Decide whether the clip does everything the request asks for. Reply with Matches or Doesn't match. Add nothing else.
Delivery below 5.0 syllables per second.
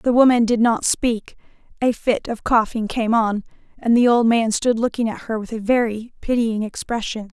Matches